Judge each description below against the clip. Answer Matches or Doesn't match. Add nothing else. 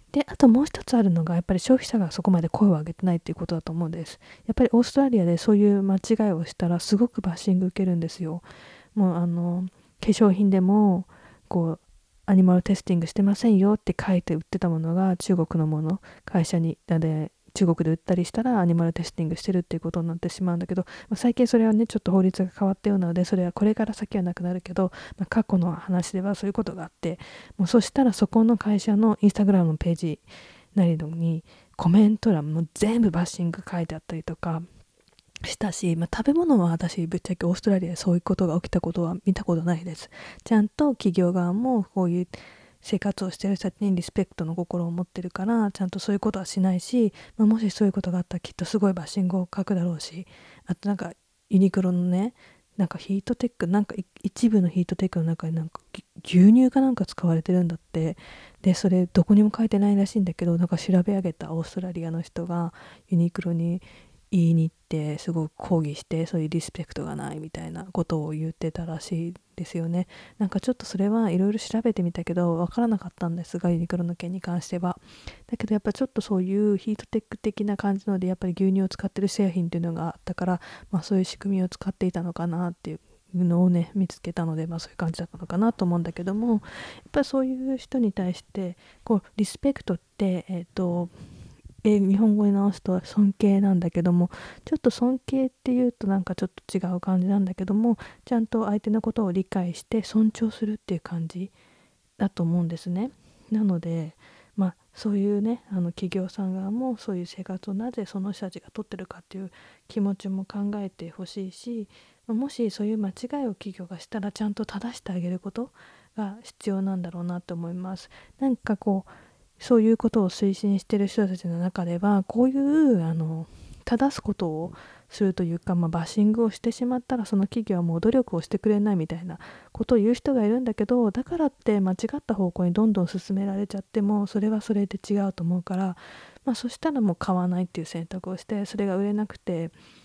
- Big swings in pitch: Doesn't match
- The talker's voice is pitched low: Doesn't match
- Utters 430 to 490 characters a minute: Matches